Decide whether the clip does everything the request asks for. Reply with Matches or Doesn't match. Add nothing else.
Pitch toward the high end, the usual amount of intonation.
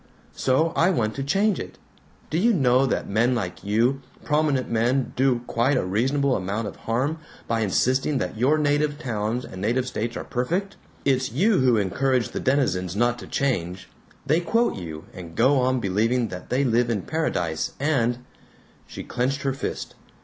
Doesn't match